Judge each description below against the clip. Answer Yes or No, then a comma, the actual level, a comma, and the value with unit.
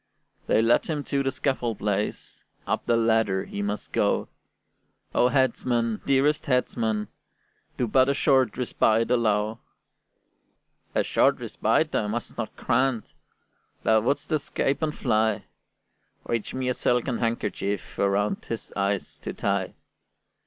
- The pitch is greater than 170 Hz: No, low, 115 Hz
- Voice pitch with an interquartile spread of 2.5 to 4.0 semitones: Yes, average, 3.5 semitones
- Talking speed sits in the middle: No, slow, 130 wpm